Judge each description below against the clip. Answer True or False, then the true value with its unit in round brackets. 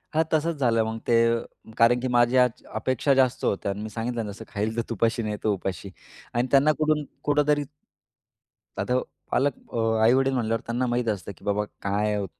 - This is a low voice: True (115 Hz)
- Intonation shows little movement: False (3.3 semitones)